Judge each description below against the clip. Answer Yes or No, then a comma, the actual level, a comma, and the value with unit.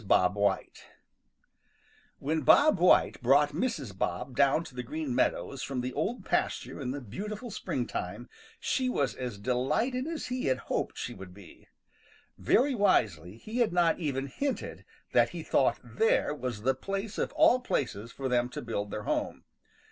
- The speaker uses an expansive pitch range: Yes, wide, 8.9 semitones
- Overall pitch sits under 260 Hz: Yes, low, 135 Hz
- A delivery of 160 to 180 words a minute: Yes, average, 165 wpm